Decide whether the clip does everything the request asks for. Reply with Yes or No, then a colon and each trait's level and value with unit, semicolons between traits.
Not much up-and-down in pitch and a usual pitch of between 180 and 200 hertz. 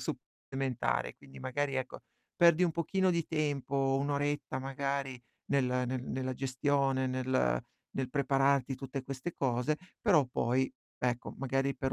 No: narrow, 1.7 semitones; low, 135 Hz